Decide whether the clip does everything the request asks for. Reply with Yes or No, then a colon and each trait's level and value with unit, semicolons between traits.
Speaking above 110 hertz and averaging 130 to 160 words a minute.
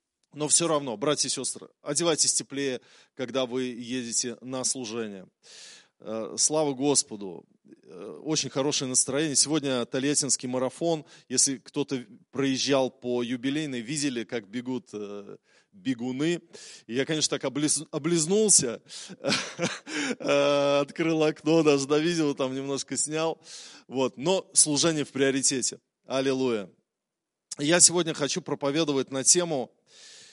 No: medium, 140 Hz; slow, 110 wpm